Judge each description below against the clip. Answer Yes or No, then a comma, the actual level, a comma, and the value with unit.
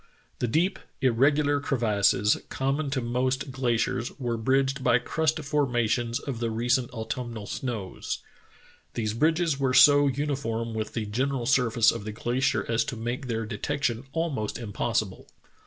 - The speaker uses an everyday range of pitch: Yes, average, 3.3 semitones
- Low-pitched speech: Yes, low, 125 Hz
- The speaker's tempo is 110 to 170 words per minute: Yes, average, 150 wpm